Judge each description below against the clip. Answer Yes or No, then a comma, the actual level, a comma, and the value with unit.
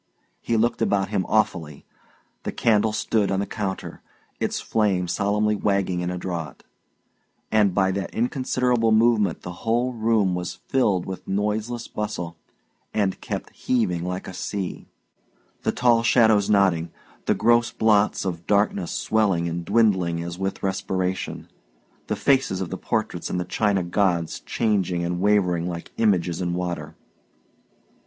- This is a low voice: Yes, low, 100 Hz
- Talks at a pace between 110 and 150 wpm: Yes, average, 145 wpm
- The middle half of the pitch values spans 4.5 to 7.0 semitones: No, average, 3.6 semitones